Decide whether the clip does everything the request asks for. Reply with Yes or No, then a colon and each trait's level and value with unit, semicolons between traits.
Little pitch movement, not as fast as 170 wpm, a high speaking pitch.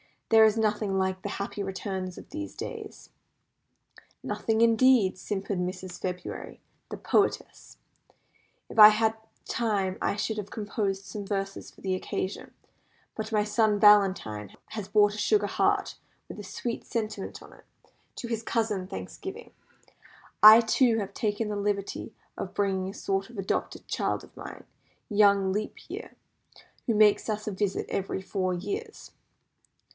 Yes: narrow, 2.3 semitones; average, 150 wpm; high, 205 Hz